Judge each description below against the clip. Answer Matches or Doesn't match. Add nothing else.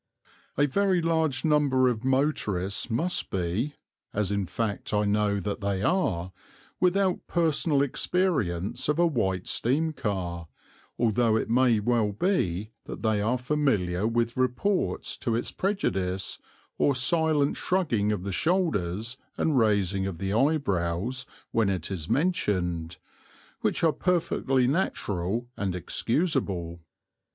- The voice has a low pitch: Matches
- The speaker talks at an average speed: Doesn't match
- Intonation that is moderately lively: Doesn't match